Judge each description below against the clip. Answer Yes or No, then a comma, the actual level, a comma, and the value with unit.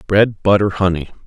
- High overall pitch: No, very low, 95 Hz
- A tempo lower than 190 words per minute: Yes, average, 140 wpm